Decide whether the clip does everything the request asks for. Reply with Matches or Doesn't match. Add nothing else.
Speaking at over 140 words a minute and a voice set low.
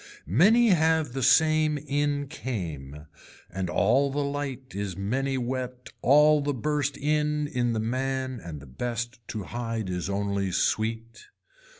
Doesn't match